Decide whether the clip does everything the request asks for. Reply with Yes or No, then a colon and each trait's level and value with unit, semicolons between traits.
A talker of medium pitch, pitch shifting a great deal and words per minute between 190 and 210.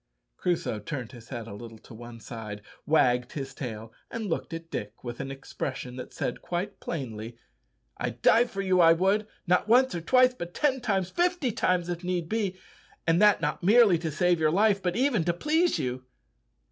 Yes: medium, 170 Hz; wide, 8.5 semitones; average, 195 wpm